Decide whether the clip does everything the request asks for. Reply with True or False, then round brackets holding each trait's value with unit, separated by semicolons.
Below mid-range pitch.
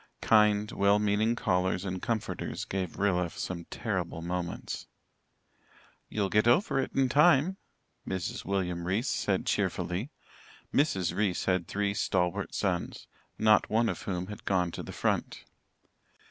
True (100 Hz)